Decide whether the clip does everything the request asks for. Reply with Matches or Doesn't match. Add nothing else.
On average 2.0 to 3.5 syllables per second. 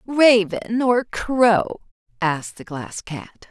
Matches